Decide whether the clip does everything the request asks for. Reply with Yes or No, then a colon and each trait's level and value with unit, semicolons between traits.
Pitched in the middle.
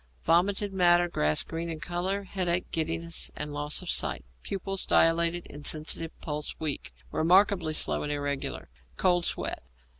Yes: medium, 170 Hz